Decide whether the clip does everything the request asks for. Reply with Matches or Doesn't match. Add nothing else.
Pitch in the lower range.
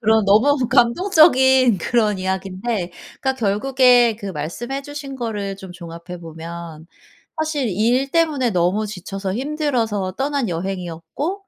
Doesn't match